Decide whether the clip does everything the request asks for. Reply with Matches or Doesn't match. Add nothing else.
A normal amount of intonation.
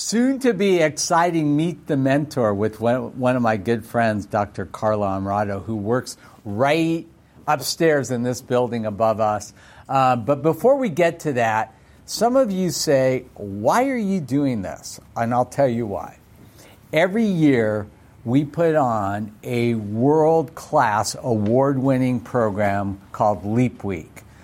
Doesn't match